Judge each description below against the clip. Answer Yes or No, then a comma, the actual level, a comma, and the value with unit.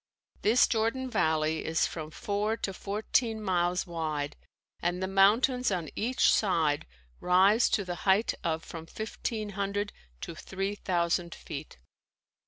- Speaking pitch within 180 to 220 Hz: Yes, high, 190 Hz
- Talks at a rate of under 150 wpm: Yes, slow, 135 wpm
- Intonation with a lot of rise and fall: No, average, 4.1 semitones